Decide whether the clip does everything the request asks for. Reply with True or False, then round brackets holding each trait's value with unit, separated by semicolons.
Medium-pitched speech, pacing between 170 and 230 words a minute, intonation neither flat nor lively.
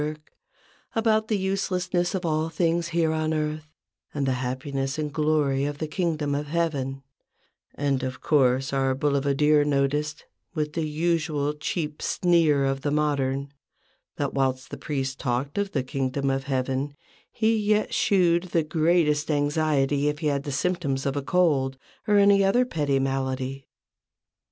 False (150 Hz; 150 wpm; 3.4 semitones)